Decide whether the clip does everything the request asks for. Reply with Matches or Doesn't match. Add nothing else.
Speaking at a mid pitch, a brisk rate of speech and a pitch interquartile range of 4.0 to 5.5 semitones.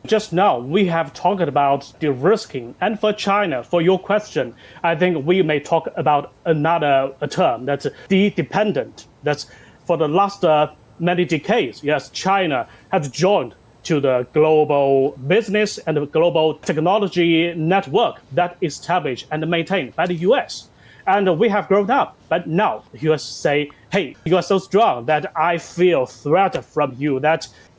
Doesn't match